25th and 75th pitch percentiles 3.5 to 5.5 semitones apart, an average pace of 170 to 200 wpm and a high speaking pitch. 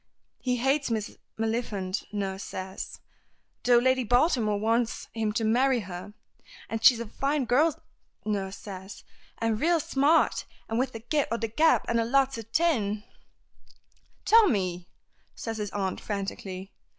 No: average, 4.2 semitones; average, 145 wpm; high, 225 Hz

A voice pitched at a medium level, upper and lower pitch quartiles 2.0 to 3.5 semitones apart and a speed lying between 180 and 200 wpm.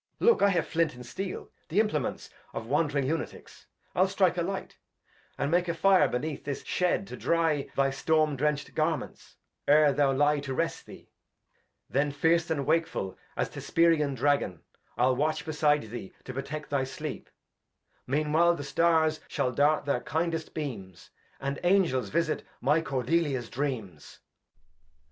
No: medium, 150 Hz; average, 3.2 semitones; average, 160 wpm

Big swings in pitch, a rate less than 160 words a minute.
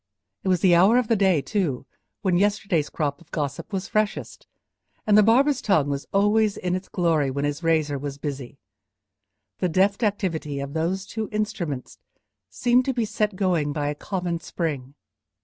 No: wide, 5.9 semitones; average, 175 wpm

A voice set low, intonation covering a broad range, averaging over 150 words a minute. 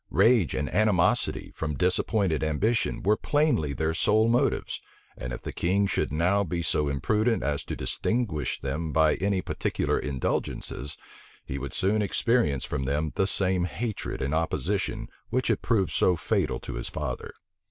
Yes: very low, 90 Hz; wide, 6.2 semitones; average, 160 wpm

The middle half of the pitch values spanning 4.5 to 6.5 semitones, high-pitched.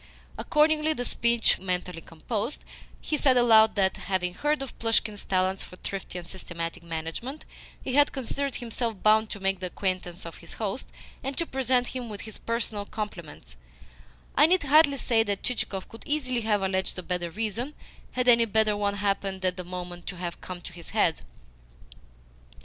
Yes: average, 5.2 semitones; high, 210 Hz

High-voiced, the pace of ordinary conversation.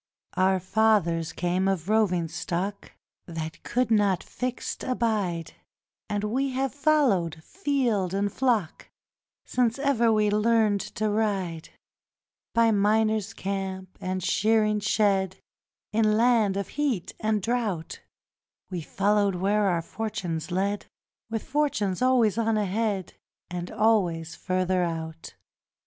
No: high, 205 Hz; slow, 120 wpm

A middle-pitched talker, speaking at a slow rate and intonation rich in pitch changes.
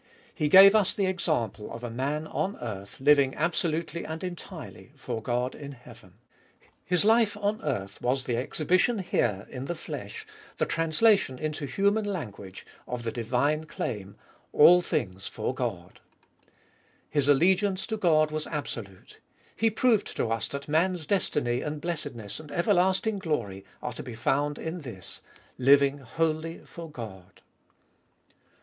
No: medium, 150 Hz; average, 155 wpm; wide, 6.5 semitones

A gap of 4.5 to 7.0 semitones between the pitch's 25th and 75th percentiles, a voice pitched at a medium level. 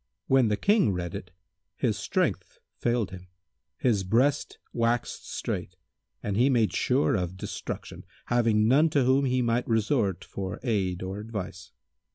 No: average, 4.8 semitones; low, 115 Hz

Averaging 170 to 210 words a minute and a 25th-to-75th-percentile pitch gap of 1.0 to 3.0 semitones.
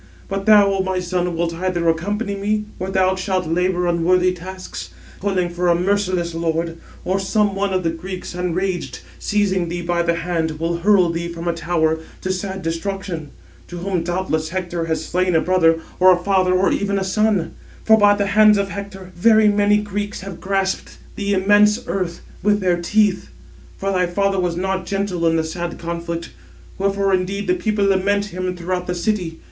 Yes: average, 185 wpm; narrow, 2.5 semitones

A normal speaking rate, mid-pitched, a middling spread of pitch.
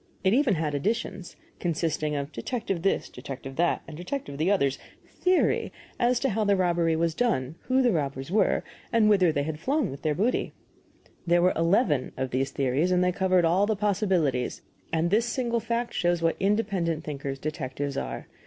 No: average, 180 wpm; medium, 175 Hz; wide, 5.8 semitones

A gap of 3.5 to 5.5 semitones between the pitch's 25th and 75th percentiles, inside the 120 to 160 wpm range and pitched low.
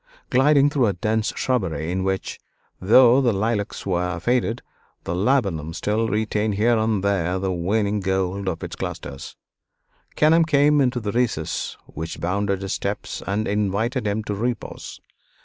Yes: average, 4.1 semitones; average, 150 wpm; low, 105 Hz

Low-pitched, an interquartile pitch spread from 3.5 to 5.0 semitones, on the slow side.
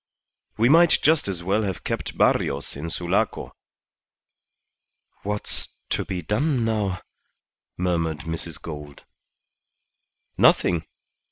Yes: very low, 90 Hz; average, 4.7 semitones; slow, 100 wpm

